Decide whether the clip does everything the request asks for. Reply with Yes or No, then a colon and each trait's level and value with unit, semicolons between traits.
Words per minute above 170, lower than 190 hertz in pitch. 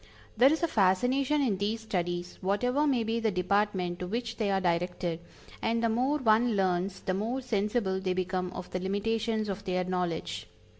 No: average, 185 wpm; high, 205 Hz